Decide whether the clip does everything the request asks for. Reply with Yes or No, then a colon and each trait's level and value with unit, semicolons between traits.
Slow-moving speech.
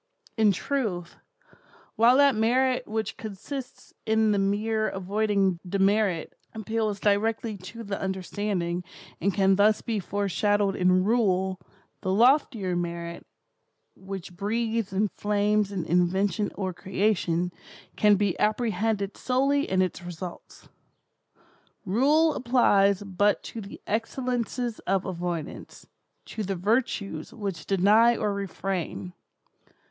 Yes: slow, 110 wpm